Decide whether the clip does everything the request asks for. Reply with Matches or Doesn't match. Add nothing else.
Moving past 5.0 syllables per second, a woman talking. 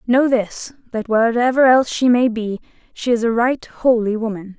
Doesn't match